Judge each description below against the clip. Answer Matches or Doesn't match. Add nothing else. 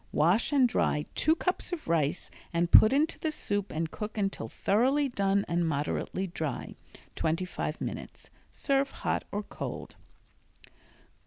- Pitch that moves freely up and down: Matches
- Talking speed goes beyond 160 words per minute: Doesn't match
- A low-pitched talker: Doesn't match